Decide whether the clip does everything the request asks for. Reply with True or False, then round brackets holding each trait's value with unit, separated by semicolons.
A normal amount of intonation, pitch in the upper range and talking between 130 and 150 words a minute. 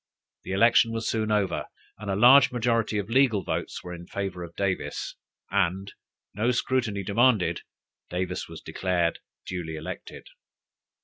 False (4.1 semitones; 100 Hz; 140 wpm)